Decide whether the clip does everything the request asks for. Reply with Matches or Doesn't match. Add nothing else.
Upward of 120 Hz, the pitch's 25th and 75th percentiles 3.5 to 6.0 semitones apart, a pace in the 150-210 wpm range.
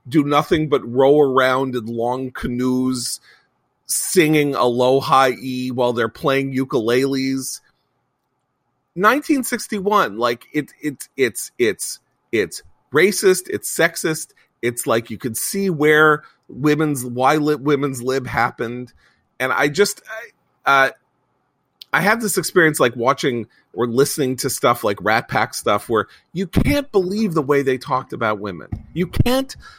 Doesn't match